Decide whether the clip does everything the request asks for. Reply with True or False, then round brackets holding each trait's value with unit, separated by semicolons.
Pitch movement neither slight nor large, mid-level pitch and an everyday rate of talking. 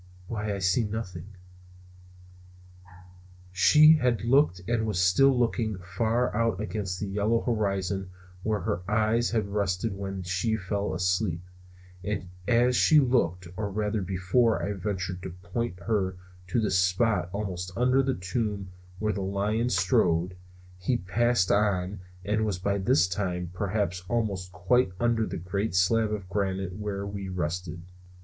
False (3.5 semitones; 100 Hz; 145 wpm)